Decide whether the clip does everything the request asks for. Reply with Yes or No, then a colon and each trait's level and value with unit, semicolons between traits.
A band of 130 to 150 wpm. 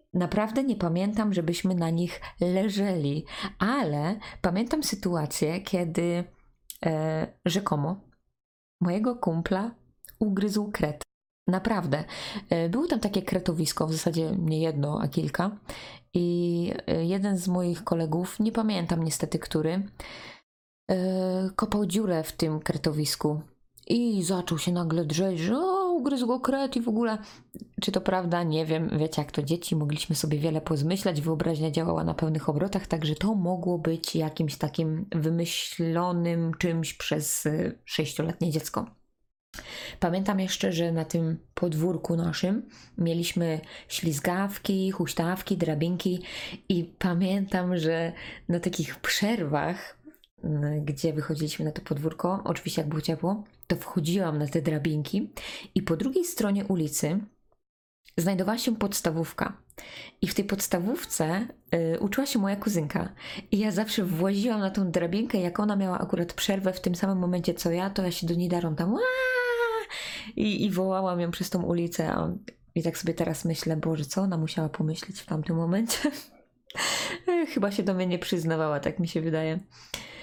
Yes: average, 140 wpm